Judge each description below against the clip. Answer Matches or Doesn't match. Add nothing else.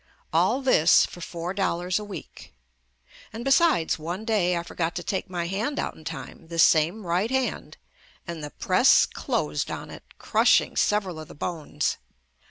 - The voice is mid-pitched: Matches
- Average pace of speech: Matches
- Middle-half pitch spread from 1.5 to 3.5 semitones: Doesn't match